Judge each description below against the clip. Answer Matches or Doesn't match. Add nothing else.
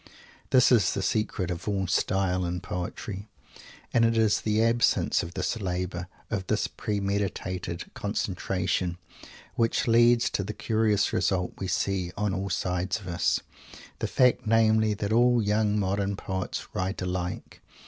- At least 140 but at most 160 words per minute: Matches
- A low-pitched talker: Matches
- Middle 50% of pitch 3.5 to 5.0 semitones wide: Doesn't match